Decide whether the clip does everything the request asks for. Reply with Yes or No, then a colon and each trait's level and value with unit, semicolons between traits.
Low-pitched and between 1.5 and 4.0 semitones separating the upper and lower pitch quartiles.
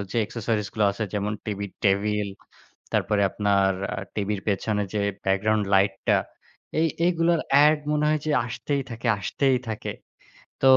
No: low, 105 Hz; average, 4.8 semitones